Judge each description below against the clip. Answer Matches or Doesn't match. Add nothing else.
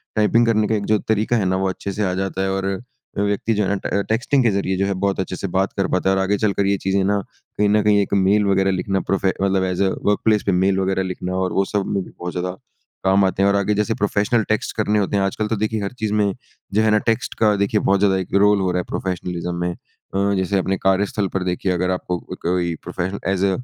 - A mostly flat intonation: Matches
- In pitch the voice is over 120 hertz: Doesn't match